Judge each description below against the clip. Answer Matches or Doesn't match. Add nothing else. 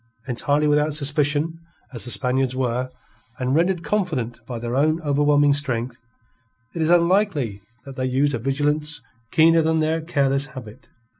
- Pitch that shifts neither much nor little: Matches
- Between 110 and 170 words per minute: Matches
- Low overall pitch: Doesn't match